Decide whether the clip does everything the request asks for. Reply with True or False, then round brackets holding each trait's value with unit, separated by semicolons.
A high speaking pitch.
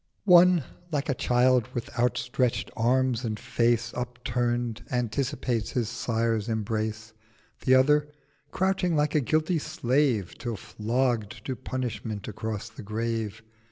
False (120 Hz)